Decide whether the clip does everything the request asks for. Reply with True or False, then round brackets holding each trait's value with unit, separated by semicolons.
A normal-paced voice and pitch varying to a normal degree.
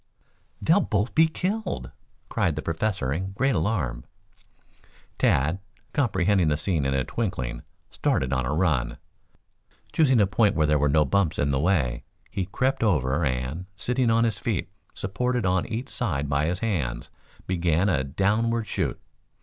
False (160 wpm; 7.3 semitones)